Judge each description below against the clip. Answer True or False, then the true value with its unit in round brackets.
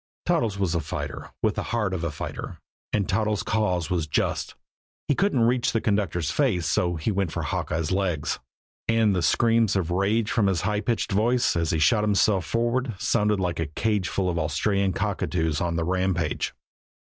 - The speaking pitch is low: True (100 Hz)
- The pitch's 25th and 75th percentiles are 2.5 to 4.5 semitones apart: True (4.2 semitones)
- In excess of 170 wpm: True (185 wpm)